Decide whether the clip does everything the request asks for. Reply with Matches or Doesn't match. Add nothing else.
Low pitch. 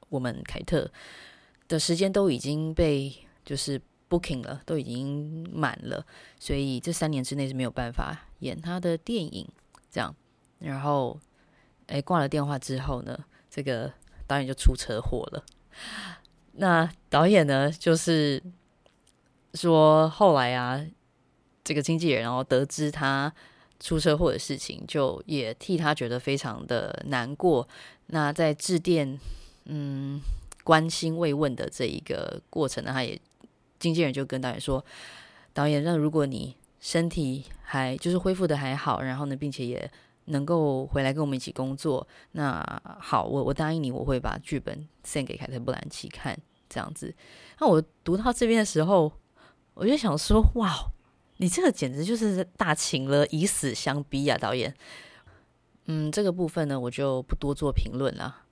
Doesn't match